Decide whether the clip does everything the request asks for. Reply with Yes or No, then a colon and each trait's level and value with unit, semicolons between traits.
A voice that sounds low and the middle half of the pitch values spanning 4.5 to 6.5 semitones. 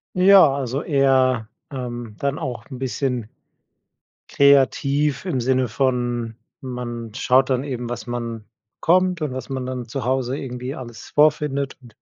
No: low, 130 Hz; narrow, 2.4 semitones